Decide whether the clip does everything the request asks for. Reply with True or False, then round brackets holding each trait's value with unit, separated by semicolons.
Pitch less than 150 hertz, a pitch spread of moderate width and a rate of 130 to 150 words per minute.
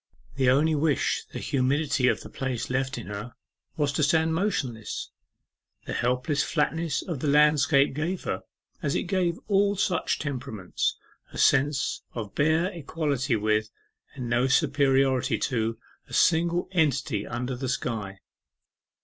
True (140 Hz; 4.2 semitones; 140 wpm)